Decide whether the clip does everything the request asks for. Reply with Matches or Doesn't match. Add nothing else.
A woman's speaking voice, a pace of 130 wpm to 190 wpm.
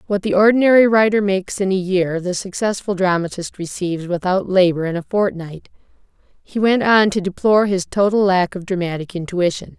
Matches